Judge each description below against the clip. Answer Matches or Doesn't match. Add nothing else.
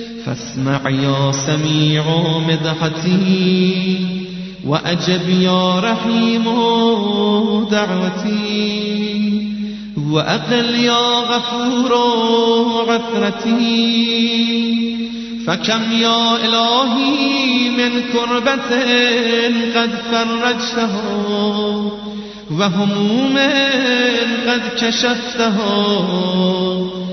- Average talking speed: Doesn't match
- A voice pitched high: Matches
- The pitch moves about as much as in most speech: Matches